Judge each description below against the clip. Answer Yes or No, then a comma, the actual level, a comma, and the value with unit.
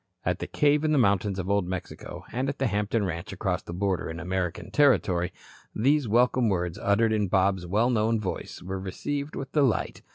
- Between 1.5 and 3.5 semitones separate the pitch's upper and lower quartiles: No, average, 5.2 semitones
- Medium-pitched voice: No, low, 100 Hz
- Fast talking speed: No, average, 195 wpm